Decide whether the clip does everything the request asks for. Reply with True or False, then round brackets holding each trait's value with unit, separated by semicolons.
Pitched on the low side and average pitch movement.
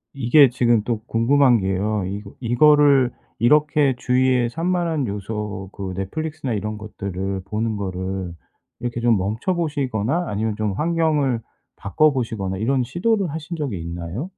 False (120 Hz; 6.4 semitones)